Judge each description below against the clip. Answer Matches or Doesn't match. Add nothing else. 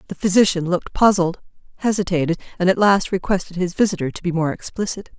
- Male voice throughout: Doesn't match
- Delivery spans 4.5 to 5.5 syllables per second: Doesn't match